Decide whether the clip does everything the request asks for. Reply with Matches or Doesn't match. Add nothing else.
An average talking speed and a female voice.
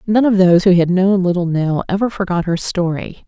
Doesn't match